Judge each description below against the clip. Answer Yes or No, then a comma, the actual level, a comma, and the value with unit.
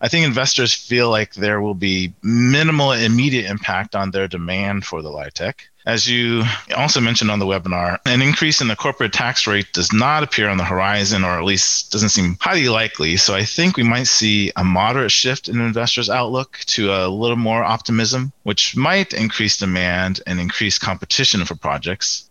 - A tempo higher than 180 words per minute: Yes, average, 190 wpm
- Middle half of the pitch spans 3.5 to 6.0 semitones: Yes, average, 3.9 semitones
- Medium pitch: No, low, 110 Hz